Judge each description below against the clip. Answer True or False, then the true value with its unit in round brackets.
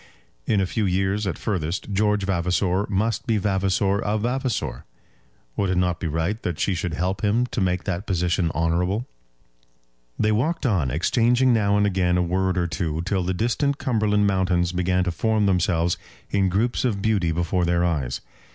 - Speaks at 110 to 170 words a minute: False (180 wpm)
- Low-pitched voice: True (95 Hz)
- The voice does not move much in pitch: False (3.0 semitones)